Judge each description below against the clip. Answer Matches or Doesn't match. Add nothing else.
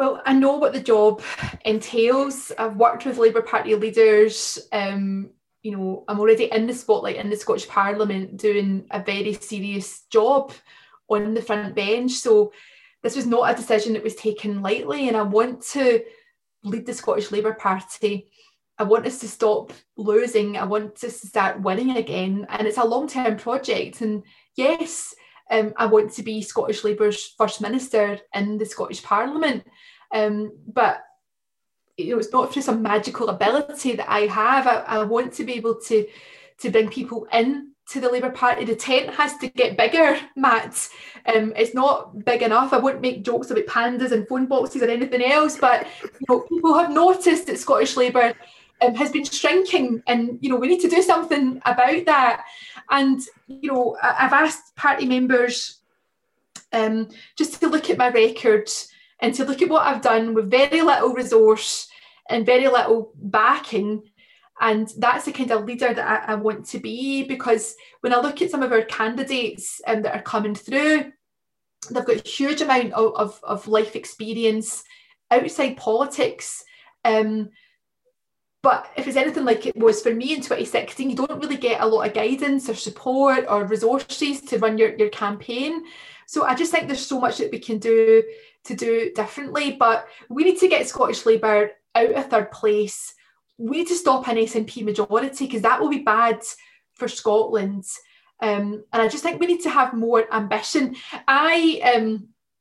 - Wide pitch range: Doesn't match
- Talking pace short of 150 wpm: Doesn't match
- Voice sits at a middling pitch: Doesn't match